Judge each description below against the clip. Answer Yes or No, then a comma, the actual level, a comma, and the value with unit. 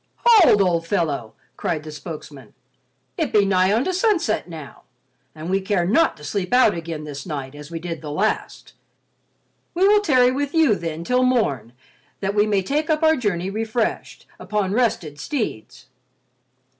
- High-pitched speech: Yes, high, 195 Hz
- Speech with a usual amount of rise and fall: No, wide, 7.8 semitones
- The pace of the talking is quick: No, average, 165 wpm